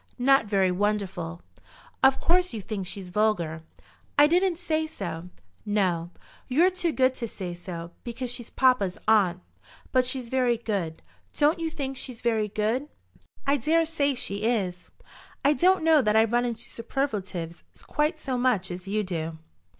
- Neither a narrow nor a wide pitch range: No, wide, 6.4 semitones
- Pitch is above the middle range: Yes, high, 230 Hz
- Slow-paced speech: No, average, 160 wpm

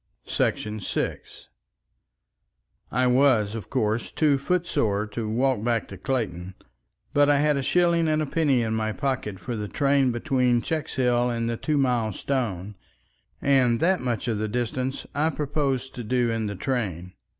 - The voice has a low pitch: Yes, low, 125 Hz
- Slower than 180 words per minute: Yes, average, 160 wpm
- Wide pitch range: No, average, 4.1 semitones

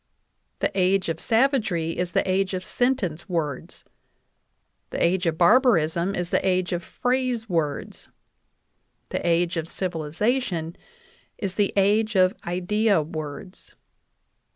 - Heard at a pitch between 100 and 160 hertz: No, medium, 180 Hz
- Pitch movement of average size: Yes, average, 4.0 semitones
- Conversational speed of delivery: No, slow, 120 wpm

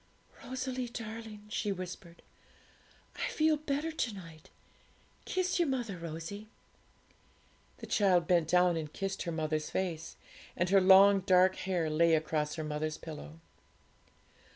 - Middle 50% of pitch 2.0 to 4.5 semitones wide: No, average, 4.9 semitones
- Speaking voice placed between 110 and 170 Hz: No, medium, 185 Hz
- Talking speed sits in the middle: No, slow, 130 wpm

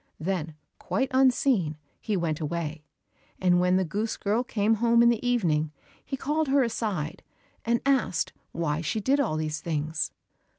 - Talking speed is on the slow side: No, average, 160 wpm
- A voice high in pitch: Yes, high, 195 Hz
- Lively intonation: Yes, wide, 7.0 semitones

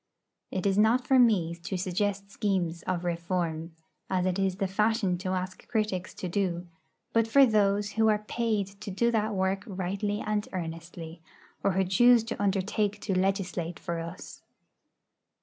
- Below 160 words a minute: No, average, 165 wpm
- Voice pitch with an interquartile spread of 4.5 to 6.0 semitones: No, average, 2.8 semitones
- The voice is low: No, high, 195 Hz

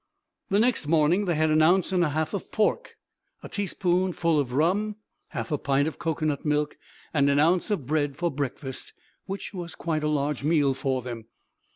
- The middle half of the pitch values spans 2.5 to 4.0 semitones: Yes, average, 3.6 semitones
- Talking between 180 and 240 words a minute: Yes, average, 190 wpm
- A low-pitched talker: No, medium, 155 Hz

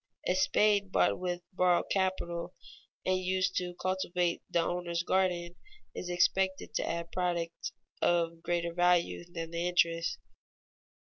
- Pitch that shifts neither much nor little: No, narrow, 1.4 semitones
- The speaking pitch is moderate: Yes, medium, 175 Hz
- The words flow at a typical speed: No, slow, 130 wpm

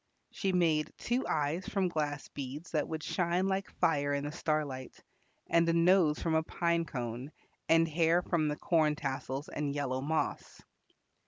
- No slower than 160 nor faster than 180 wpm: Yes, average, 165 wpm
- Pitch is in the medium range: Yes, medium, 155 Hz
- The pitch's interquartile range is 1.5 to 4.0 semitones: Yes, average, 2.8 semitones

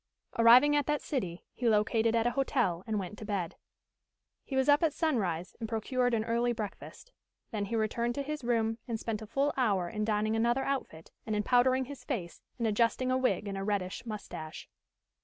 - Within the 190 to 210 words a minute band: Yes, average, 200 wpm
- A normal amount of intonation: Yes, average, 3.5 semitones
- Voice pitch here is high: Yes, high, 230 Hz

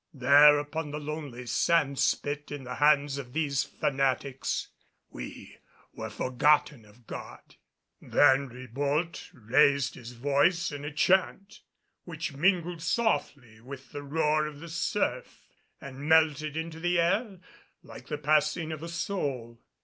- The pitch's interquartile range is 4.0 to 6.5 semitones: No, average, 3.0 semitones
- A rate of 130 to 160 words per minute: Yes, slow, 135 wpm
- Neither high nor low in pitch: Yes, medium, 145 Hz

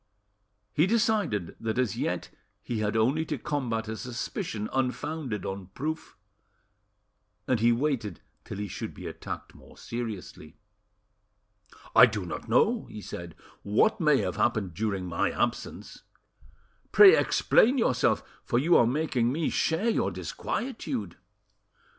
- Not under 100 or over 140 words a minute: Yes, slow, 135 wpm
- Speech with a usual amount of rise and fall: No, wide, 6.6 semitones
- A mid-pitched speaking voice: No, low, 120 Hz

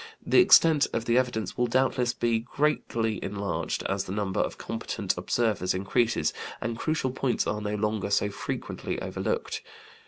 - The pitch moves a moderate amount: Yes, average, 3.4 semitones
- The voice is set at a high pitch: No, low, 115 Hz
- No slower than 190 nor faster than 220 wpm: No, average, 155 wpm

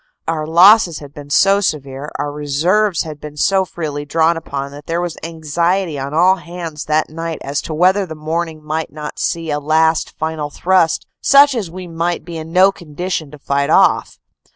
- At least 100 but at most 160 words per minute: No, average, 190 wpm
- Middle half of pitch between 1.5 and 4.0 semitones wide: Yes, average, 2.8 semitones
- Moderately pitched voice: Yes, medium, 160 Hz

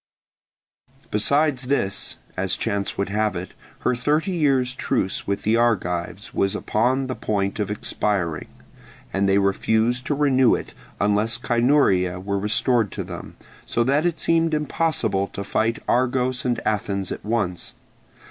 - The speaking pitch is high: No, low, 115 Hz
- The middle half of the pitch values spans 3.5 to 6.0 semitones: Yes, average, 4.7 semitones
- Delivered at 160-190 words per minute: No, average, 145 wpm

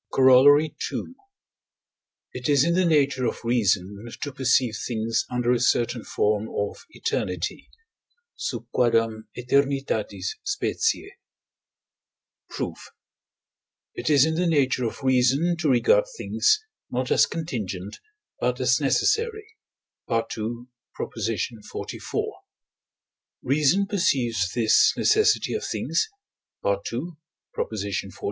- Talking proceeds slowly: Yes, slow, 105 wpm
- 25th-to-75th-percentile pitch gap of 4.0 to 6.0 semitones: Yes, wide, 5.4 semitones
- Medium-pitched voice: No, low, 125 Hz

